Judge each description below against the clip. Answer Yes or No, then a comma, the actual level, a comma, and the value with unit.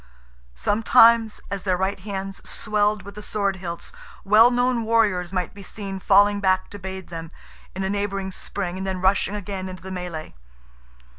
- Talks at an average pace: Yes, average, 170 wpm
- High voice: Yes, high, 195 Hz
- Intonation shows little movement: Yes, narrow, 1.7 semitones